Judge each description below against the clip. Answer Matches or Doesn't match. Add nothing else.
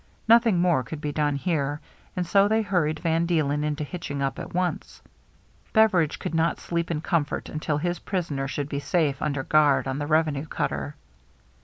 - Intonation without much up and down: Doesn't match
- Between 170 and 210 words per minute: Matches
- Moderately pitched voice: Matches